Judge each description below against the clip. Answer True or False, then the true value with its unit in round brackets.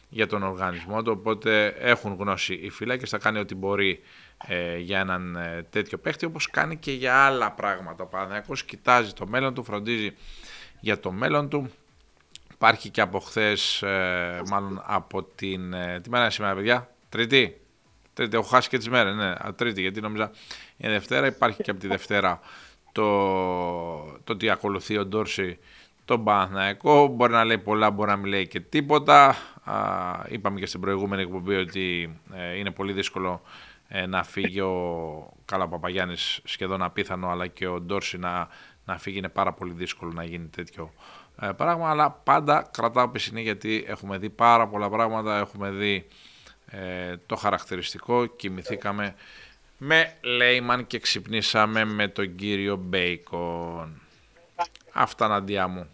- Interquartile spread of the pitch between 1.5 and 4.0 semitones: True (3.5 semitones)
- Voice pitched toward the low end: True (100 Hz)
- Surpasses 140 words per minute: True (150 wpm)